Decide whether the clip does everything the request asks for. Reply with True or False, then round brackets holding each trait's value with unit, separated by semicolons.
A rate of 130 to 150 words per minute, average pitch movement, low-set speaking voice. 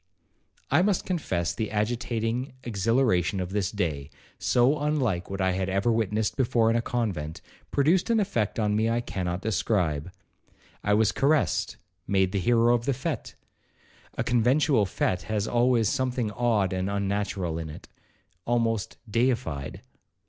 True (140 wpm; 4.4 semitones; 110 Hz)